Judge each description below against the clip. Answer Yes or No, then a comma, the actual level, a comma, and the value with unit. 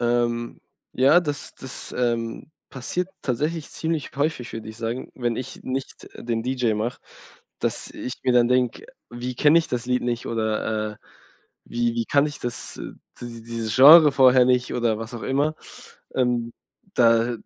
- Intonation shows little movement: Yes, narrow, 2.3 semitones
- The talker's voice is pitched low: Yes, low, 125 Hz